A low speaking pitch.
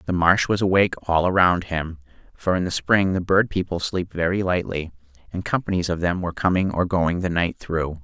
Yes: very low, 90 Hz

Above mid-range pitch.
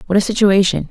Yes: high, 200 Hz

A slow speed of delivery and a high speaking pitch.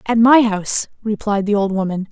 No: average, 200 wpm; high, 210 Hz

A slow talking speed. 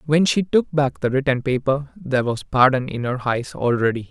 No: fast, 205 wpm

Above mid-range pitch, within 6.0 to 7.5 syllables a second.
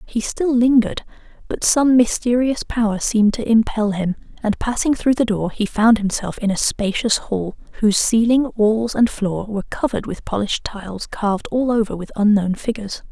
No: high, 220 Hz; 5.3 syllables/s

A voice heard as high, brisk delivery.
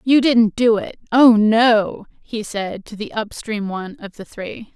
No: high, 220 Hz; average, 190 wpm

